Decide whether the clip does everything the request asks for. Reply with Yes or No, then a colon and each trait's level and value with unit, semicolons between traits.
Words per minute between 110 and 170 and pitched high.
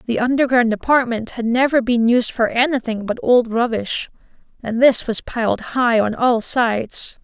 Yes: average, 165 wpm; high, 240 Hz